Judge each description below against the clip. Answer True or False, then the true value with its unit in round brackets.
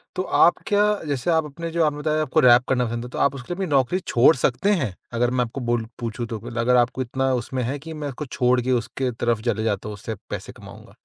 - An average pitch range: True (3.8 semitones)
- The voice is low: True (125 Hz)